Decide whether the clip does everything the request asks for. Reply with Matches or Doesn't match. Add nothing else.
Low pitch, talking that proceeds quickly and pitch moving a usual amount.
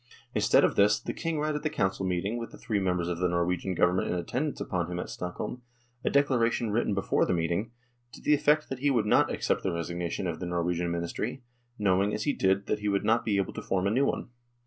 Matches